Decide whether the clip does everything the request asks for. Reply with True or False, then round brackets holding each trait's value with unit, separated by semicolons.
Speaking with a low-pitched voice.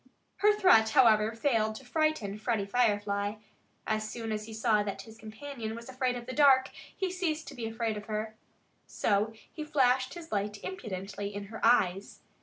False (225 Hz)